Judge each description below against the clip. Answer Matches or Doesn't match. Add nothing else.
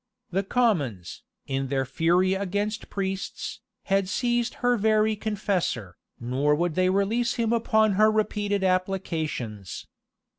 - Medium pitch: Doesn't match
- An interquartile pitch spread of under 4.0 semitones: Doesn't match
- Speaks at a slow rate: Matches